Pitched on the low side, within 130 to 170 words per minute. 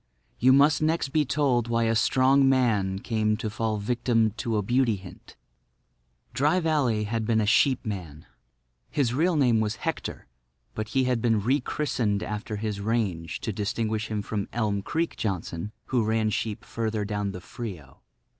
Yes: low, 110 Hz; average, 165 wpm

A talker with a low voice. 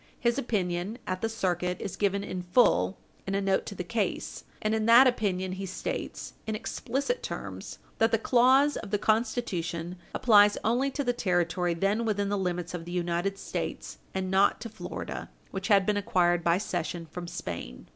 No: high, 195 Hz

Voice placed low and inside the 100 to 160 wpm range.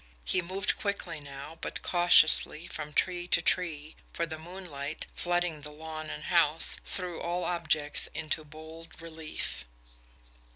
No: medium, 160 Hz; slow, 135 wpm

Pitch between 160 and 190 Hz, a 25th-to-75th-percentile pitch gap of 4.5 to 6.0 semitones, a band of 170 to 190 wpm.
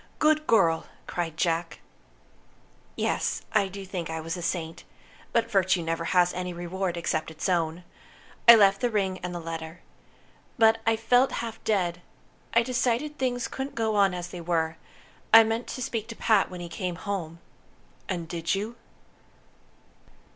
No: medium, 185 Hz; average, 4.9 semitones; average, 160 wpm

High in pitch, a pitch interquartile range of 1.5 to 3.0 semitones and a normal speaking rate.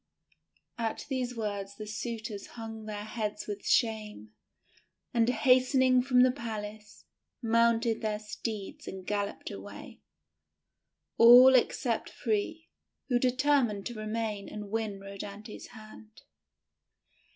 No: high, 220 Hz; narrow, 2.6 semitones; slow, 115 wpm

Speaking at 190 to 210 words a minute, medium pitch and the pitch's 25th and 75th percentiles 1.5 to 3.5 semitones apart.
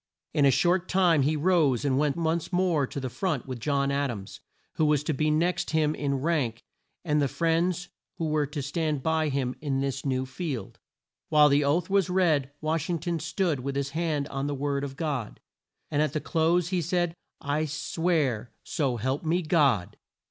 Yes: average, 200 wpm; medium, 150 Hz; average, 3.2 semitones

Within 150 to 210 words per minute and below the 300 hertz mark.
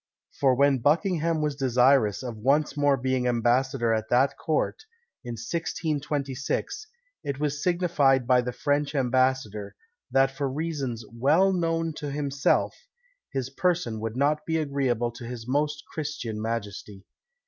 No: slow, 135 wpm; low, 135 Hz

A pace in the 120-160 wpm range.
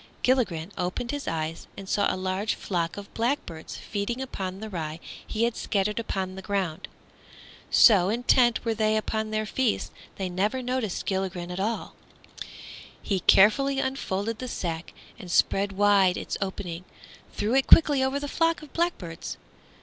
Yes: average, 155 wpm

